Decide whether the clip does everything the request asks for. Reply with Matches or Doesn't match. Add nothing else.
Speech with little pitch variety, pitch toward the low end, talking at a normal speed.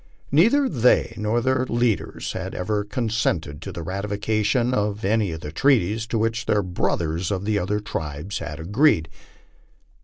Doesn't match